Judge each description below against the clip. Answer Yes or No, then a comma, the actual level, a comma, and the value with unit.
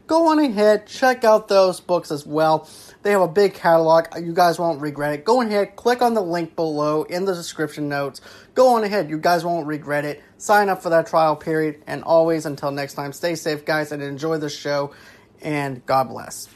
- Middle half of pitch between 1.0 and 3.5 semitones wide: No, average, 4.4 semitones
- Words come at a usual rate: No, fast, 215 wpm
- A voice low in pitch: No, medium, 165 Hz